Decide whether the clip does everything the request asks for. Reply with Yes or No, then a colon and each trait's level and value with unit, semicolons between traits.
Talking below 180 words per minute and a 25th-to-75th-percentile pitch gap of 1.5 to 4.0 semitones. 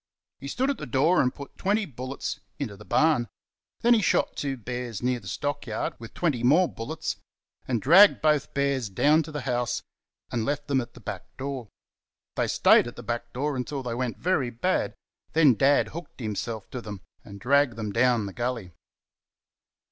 No: average, 190 wpm; average, 3.7 semitones